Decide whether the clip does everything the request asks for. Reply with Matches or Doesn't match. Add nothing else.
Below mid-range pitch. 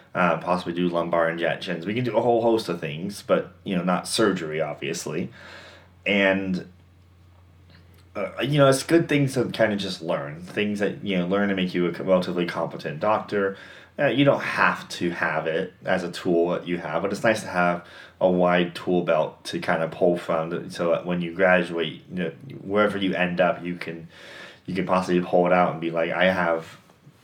Matches